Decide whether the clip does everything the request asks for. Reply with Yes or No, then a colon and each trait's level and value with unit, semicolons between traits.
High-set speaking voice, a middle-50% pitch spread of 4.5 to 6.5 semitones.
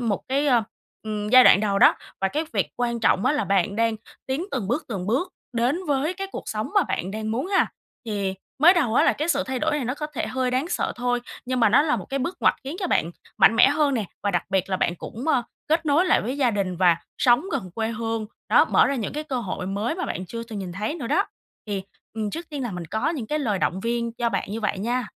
Yes: high, 235 Hz; average, 5.2 semitones